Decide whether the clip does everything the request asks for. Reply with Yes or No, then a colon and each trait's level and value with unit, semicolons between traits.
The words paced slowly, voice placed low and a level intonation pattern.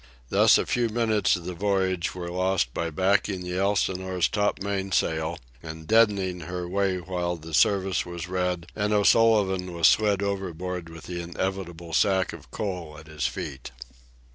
No: average, 160 wpm; very low, 90 Hz; narrow, 2.3 semitones